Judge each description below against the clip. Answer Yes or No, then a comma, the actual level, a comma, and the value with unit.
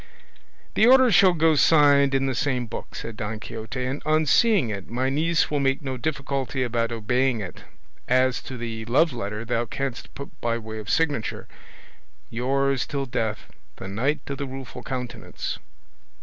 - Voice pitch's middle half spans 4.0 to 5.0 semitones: No, average, 3.5 semitones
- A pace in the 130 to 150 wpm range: No, average, 165 wpm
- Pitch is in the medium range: No, low, 130 Hz